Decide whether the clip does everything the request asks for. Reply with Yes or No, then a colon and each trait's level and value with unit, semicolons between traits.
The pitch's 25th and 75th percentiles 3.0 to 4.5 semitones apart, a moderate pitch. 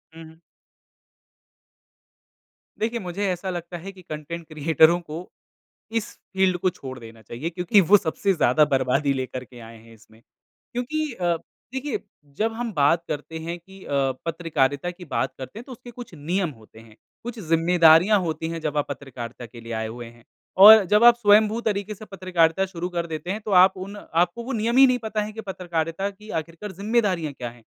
No: wide, 5.6 semitones; medium, 175 Hz